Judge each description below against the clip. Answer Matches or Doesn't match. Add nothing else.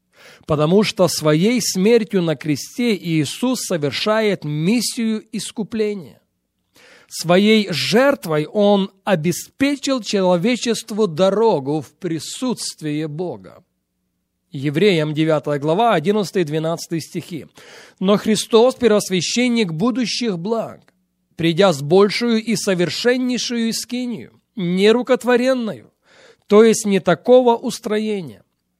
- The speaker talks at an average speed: Doesn't match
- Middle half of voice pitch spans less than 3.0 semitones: Doesn't match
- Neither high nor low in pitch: Doesn't match